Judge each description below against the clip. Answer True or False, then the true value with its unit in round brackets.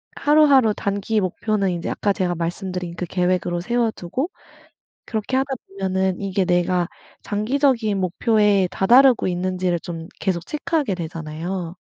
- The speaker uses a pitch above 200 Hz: False (190 Hz)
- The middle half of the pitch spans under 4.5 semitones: True (4.0 semitones)